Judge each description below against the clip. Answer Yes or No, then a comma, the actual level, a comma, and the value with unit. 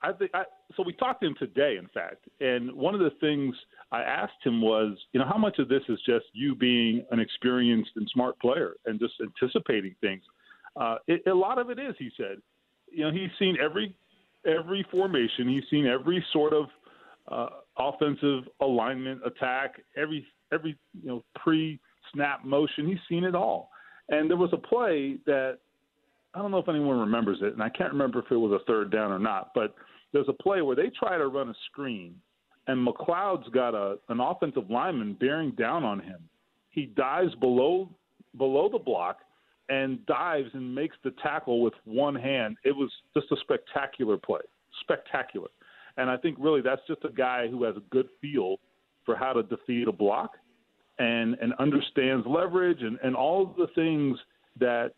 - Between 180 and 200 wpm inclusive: Yes, average, 190 wpm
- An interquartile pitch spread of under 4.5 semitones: No, wide, 5.5 semitones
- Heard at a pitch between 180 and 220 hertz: No, medium, 140 Hz